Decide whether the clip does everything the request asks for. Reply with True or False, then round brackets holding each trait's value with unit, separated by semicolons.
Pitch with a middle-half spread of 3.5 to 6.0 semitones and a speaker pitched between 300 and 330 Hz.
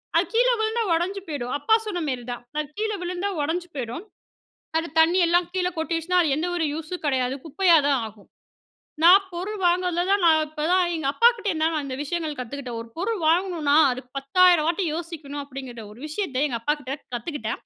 True (4.3 semitones; 320 Hz)